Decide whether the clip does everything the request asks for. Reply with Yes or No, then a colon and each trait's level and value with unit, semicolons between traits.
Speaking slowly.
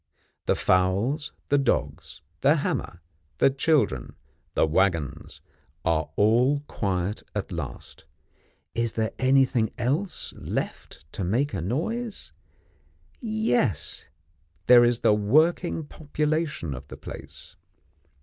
Yes: slow, 105 wpm